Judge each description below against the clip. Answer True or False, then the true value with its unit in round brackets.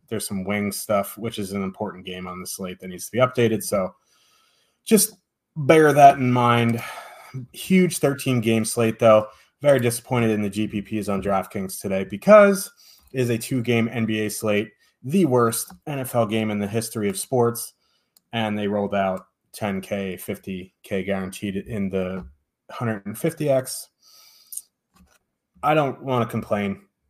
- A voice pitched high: False (110 Hz)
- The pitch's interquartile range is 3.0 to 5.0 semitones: True (4.0 semitones)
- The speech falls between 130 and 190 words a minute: True (150 wpm)